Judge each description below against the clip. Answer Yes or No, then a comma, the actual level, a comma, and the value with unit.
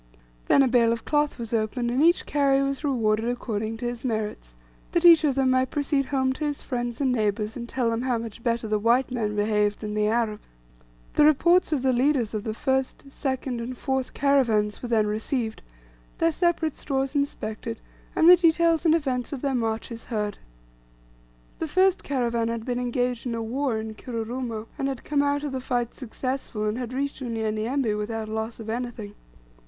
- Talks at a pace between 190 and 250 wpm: Yes, average, 195 wpm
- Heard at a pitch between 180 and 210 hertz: No, high, 245 Hz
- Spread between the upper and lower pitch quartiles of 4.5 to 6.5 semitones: No, average, 3.6 semitones